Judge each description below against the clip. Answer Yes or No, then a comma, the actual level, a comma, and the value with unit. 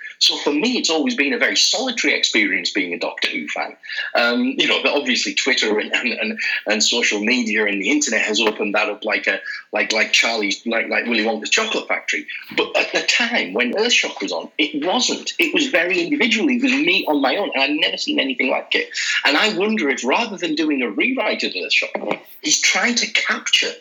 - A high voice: Yes, very high, 255 Hz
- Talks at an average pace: No, fast, 215 wpm